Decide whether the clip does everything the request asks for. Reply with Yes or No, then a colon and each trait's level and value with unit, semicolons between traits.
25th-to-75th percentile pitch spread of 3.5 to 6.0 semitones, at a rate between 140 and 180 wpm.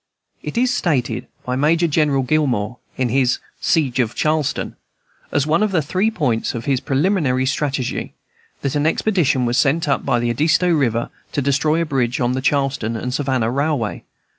Yes: average, 3.8 semitones; average, 170 wpm